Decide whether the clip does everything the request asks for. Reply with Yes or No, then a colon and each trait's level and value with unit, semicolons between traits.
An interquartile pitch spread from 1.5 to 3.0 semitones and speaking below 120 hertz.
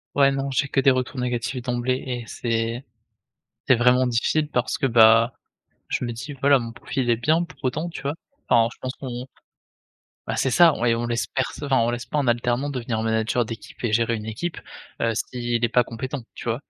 No: narrow, 2.5 semitones; low, 125 Hz